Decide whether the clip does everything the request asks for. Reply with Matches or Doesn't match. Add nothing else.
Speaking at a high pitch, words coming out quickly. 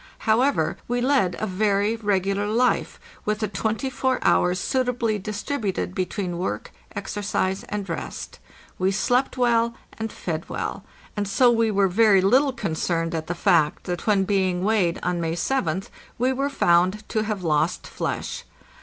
Doesn't match